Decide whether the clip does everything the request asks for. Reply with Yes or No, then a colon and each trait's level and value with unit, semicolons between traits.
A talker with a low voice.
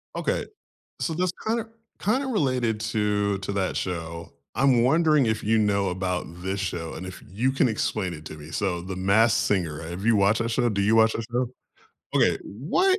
Yes: low, 105 Hz